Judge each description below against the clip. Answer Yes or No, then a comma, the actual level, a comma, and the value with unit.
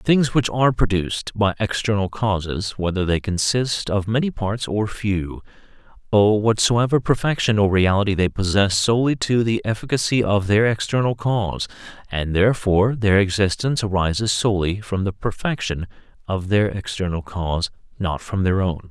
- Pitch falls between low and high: No, low, 105 Hz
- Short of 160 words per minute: Yes, average, 150 wpm